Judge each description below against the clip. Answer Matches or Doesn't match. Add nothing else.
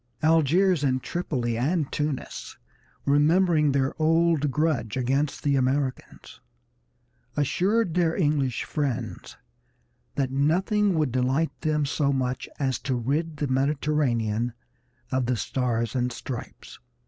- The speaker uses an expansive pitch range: Doesn't match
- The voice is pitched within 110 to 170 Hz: Matches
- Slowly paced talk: Matches